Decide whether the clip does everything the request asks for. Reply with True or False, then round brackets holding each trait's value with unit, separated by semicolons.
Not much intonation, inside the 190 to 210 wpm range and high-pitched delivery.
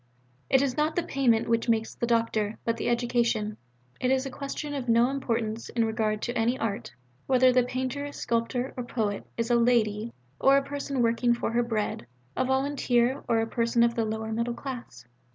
True (2.3 semitones; 195 wpm; 235 Hz)